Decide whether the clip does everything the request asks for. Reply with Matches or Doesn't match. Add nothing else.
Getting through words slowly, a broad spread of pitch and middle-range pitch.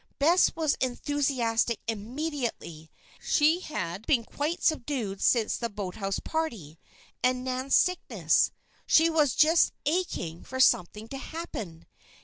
Doesn't match